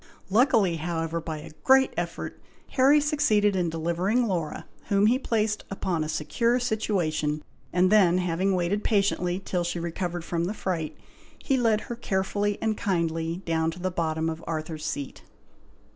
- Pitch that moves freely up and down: No, average, 4.3 semitones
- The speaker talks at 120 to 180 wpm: Yes, average, 160 wpm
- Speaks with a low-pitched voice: No, medium, 180 Hz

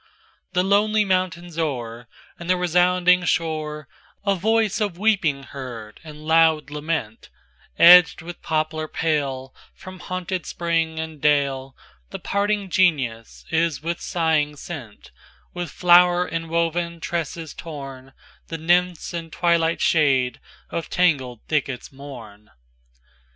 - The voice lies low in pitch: No, medium, 165 Hz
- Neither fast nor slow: No, slow, 100 wpm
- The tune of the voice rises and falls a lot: No, average, 3.8 semitones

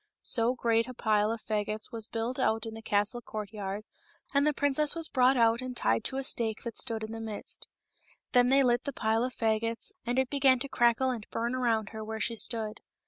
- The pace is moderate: No, fast, 220 wpm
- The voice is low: No, high, 230 Hz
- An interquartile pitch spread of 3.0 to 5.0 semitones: No, narrow, 2.6 semitones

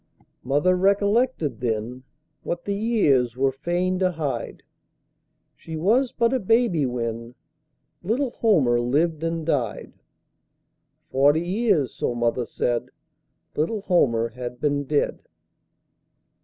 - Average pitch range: No, wide, 7.7 semitones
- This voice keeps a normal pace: No, slow, 115 wpm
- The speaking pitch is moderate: Yes, medium, 155 Hz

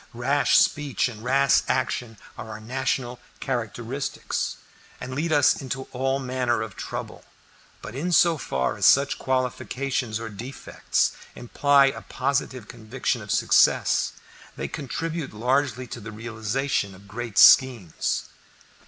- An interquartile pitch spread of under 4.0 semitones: Yes, average, 3.5 semitones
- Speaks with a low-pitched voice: Yes, low, 125 Hz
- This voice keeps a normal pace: No, slow, 130 wpm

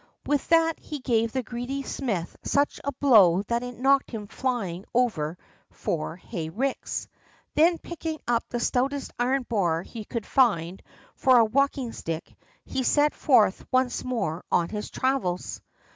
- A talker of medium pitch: No, high, 245 Hz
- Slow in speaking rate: No, average, 155 wpm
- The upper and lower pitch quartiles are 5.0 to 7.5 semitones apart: Yes, wide, 5.5 semitones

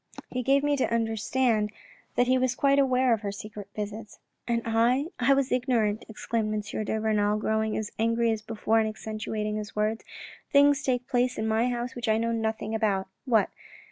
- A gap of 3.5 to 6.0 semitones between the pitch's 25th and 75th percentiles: No, narrow, 2.6 semitones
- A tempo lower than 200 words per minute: No, fast, 205 wpm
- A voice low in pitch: No, high, 225 Hz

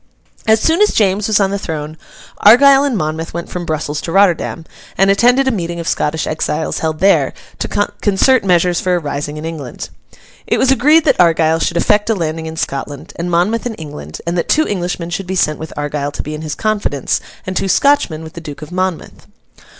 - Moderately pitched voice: Yes, medium, 175 Hz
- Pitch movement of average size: Yes, average, 4.6 semitones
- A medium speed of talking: No, fast, 210 wpm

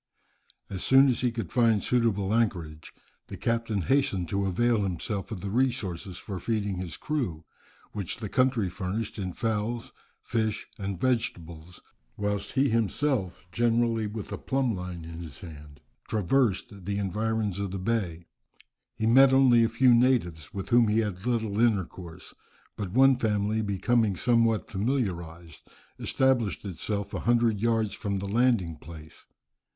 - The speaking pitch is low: Yes, low, 105 Hz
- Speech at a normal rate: Yes, average, 150 wpm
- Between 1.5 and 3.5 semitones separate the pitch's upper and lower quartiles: No, average, 4.1 semitones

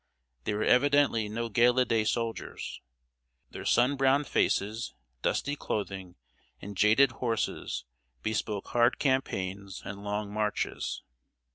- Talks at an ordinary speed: No, slow, 115 wpm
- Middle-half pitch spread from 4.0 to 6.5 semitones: No, average, 3.5 semitones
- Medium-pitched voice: No, low, 110 Hz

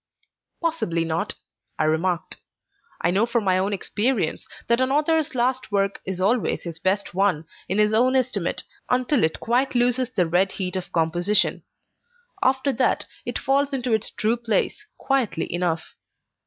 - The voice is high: Yes, high, 210 Hz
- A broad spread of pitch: Yes, wide, 5.9 semitones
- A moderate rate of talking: Yes, average, 155 wpm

